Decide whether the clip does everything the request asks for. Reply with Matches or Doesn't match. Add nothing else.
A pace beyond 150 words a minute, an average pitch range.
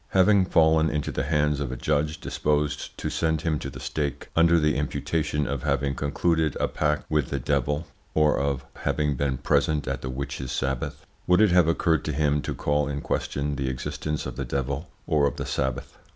Doesn't match